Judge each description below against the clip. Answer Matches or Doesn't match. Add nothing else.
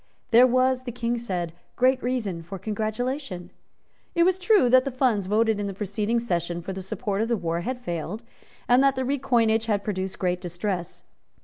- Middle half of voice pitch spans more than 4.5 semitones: Matches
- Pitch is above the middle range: Matches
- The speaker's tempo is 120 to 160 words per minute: Doesn't match